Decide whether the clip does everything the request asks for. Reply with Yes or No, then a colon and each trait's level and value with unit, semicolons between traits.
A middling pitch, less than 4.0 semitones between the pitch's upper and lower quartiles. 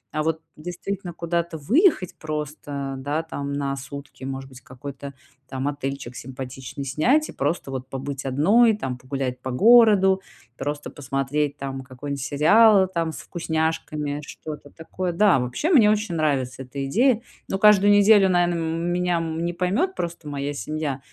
No: medium, 155 Hz; average, 4.7 semitones